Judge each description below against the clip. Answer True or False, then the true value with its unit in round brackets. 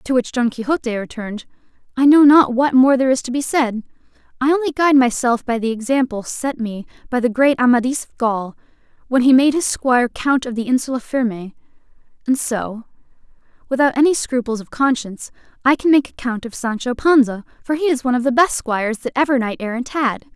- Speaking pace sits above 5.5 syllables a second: True (5.8 syllables/s)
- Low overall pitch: False (250 Hz)